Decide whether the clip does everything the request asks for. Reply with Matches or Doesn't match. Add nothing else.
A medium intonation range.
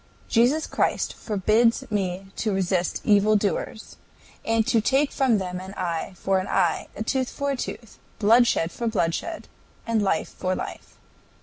Matches